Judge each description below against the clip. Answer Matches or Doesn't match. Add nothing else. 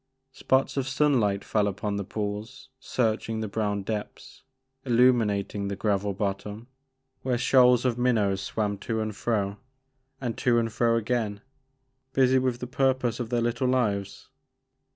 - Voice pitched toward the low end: Matches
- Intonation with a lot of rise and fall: Doesn't match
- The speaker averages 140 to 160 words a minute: Matches